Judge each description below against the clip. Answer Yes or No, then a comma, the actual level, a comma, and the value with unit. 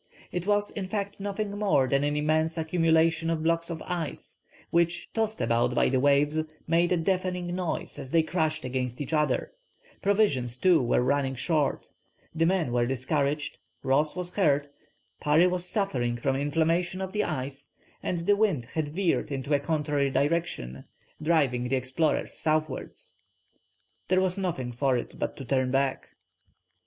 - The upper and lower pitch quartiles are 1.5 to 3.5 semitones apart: No, average, 4.6 semitones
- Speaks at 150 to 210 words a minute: Yes, average, 160 wpm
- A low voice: No, medium, 155 Hz